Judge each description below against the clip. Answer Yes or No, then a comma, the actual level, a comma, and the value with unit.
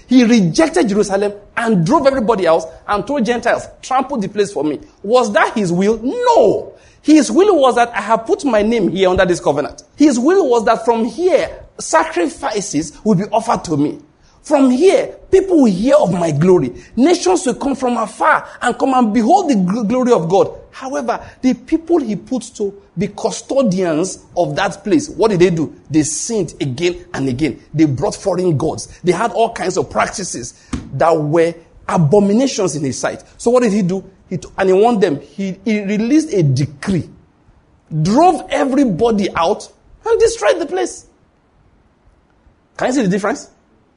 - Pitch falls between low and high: No, high, 225 Hz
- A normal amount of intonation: No, wide, 6.9 semitones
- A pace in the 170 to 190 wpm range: Yes, average, 180 wpm